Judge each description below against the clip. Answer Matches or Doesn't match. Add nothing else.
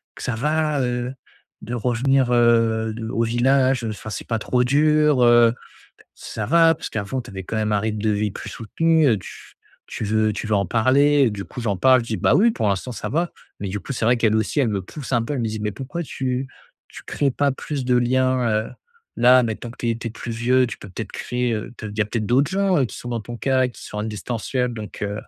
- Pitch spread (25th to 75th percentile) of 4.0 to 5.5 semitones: Doesn't match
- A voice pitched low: Matches